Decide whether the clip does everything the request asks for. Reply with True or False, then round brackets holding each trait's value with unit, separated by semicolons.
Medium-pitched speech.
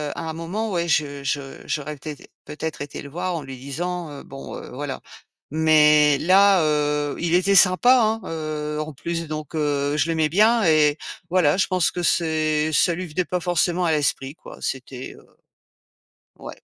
True (155 Hz)